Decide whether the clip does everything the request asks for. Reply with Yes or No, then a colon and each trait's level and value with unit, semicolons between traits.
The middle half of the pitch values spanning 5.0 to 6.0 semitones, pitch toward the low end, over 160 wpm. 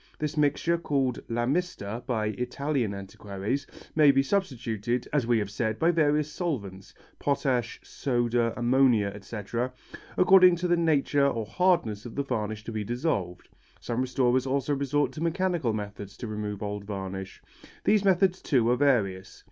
No: wide, 5.6 semitones; low, 125 Hz; average, 155 wpm